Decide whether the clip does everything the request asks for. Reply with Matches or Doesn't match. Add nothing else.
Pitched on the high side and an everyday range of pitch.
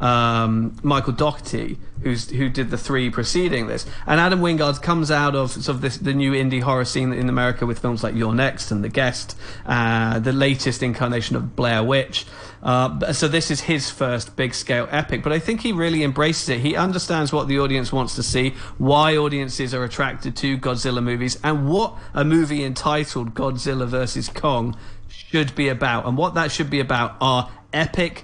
Doesn't match